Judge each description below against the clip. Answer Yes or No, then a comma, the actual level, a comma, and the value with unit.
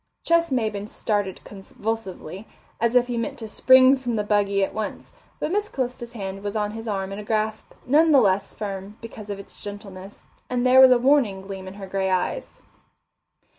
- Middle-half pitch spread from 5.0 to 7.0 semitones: No, average, 3.9 semitones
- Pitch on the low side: No, high, 215 Hz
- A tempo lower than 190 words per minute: No, average, 195 wpm